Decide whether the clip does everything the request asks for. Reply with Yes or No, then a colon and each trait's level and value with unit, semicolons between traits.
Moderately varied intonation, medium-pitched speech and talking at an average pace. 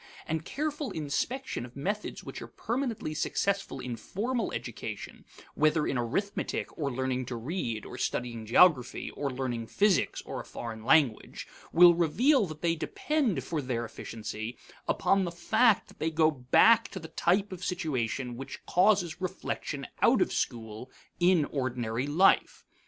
No: wide, 7.4 semitones; medium, 155 Hz; average, 155 wpm